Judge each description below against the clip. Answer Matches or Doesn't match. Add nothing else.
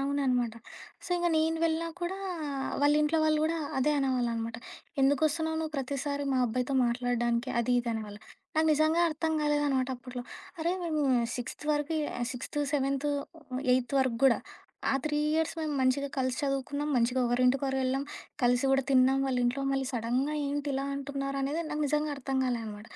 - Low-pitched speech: Doesn't match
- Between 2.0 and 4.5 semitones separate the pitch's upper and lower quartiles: Matches